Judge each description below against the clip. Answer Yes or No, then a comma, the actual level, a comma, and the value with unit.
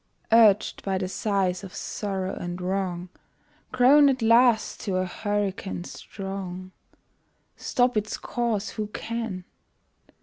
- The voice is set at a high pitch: Yes, high, 200 Hz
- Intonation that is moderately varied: Yes, average, 3.4 semitones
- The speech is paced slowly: Yes, slow, 115 wpm